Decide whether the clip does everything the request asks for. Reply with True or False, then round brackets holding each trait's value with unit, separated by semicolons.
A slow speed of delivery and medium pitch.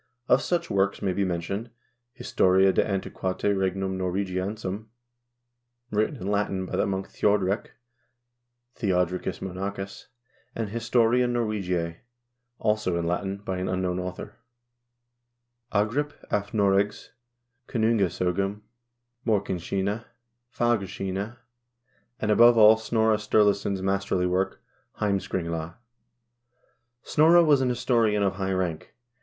False (110 wpm; 100 Hz)